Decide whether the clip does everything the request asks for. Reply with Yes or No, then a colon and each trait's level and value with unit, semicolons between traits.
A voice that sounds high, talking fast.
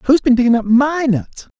Yes: very high, 250 Hz; fast, 225 wpm